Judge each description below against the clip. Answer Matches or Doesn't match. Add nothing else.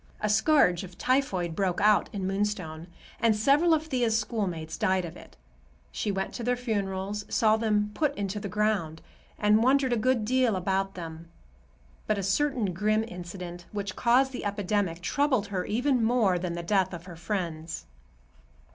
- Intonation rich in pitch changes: Doesn't match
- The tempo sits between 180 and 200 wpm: Doesn't match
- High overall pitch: Matches